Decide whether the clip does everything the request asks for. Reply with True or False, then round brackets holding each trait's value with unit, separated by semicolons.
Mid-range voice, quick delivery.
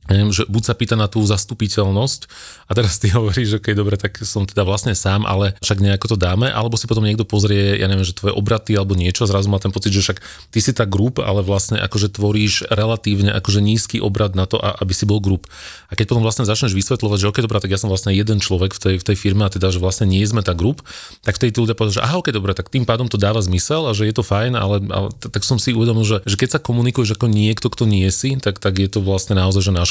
False (105 Hz; 265 wpm)